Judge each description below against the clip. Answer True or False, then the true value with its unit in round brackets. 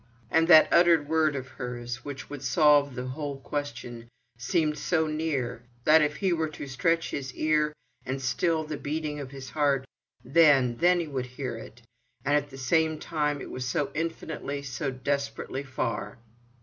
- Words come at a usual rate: True (170 wpm)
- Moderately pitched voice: True (145 Hz)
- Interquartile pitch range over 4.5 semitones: False (3.2 semitones)